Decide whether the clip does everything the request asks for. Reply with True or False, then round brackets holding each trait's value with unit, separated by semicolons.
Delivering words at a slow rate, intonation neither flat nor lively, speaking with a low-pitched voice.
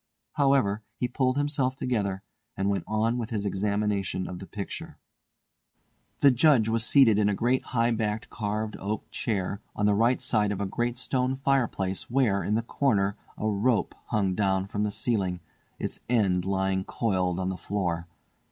False (175 wpm; 3.7 semitones; 105 Hz)